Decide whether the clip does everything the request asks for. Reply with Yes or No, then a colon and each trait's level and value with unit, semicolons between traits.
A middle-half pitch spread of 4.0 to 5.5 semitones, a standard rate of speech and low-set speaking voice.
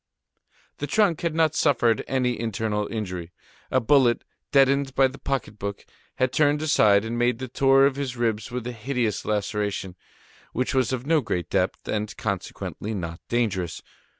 Yes: average, 4.4 semitones; average, 165 wpm; low, 120 Hz